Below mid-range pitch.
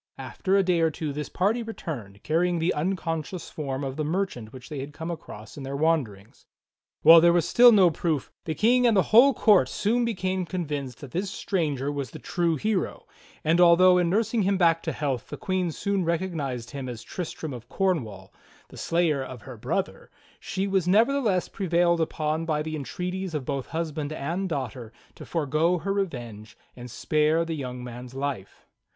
No: medium, 165 Hz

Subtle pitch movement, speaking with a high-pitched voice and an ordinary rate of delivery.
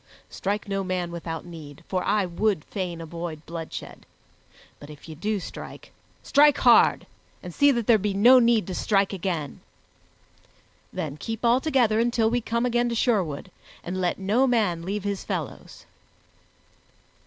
No: average, 5.3 semitones; high, 200 Hz; average, 155 wpm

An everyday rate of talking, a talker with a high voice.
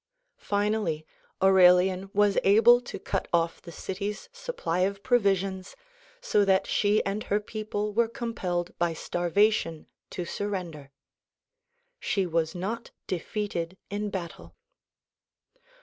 No: slow, 120 wpm; high, 195 Hz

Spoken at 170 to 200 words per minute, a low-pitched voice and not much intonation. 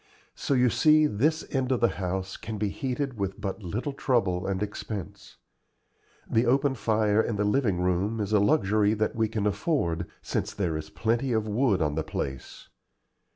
No: average, 180 wpm; low, 110 Hz; average, 4.4 semitones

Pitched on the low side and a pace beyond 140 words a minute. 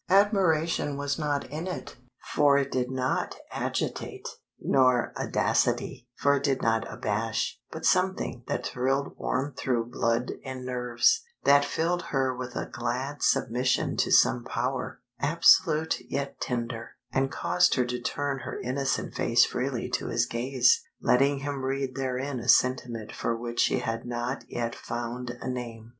Yes: low, 130 Hz; average, 150 wpm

